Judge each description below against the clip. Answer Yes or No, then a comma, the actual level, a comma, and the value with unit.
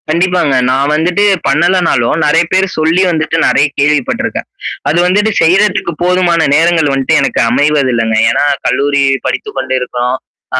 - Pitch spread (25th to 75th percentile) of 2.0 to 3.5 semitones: No, average, 4.0 semitones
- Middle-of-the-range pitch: Yes, medium, 155 Hz